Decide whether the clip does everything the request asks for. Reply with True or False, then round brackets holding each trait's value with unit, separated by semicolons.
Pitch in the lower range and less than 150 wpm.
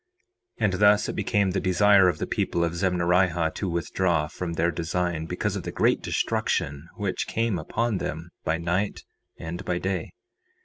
False (90 Hz; 175 wpm)